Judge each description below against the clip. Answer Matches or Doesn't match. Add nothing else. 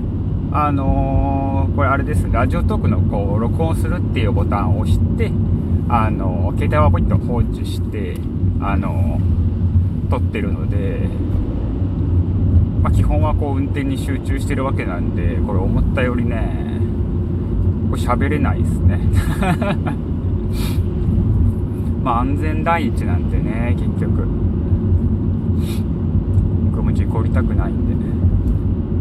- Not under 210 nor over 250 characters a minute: Matches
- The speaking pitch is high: Doesn't match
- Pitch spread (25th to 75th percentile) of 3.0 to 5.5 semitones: Doesn't match